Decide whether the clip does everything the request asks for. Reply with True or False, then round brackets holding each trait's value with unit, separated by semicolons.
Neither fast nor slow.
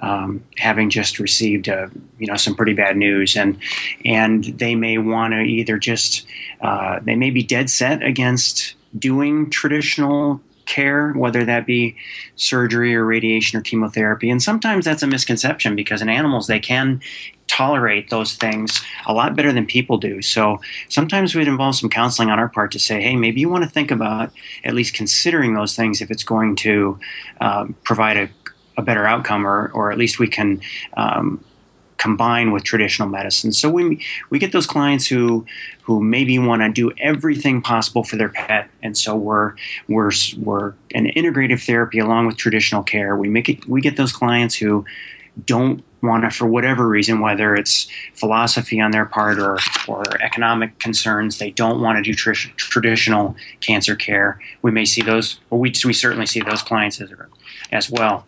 True (180 wpm)